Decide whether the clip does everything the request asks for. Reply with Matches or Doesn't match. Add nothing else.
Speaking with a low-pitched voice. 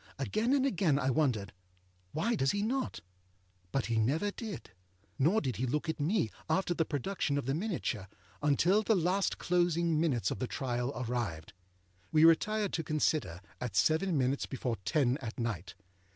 Doesn't match